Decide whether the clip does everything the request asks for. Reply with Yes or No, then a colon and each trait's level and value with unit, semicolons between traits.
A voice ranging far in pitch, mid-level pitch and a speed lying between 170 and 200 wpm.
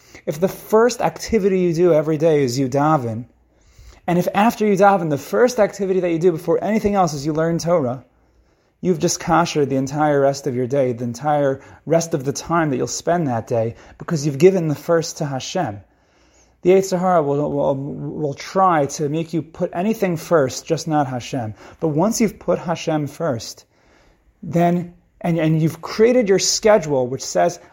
No: average, 4.7 semitones; medium, 160 Hz; average, 185 wpm